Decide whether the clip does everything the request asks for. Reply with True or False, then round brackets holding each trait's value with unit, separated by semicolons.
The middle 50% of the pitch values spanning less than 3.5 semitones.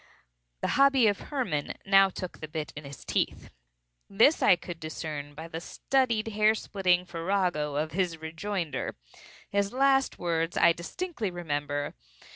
False (5.1 semitones)